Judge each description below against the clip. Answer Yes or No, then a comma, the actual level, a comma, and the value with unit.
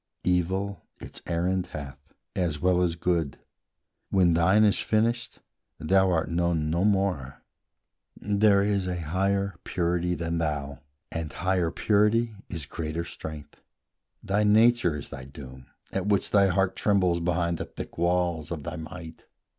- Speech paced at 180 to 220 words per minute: No, average, 145 wpm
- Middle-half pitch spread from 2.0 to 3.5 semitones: Yes, average, 3.2 semitones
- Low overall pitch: Yes, very low, 90 Hz